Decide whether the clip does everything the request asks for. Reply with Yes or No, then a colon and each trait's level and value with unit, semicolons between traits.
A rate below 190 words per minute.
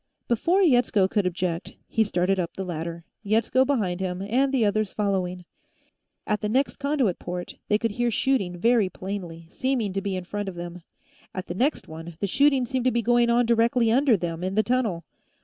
No: average, 200 wpm